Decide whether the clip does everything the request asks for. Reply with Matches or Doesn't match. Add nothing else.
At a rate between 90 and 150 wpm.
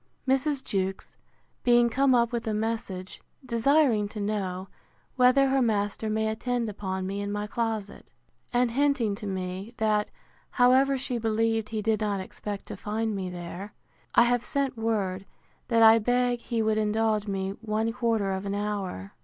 Doesn't match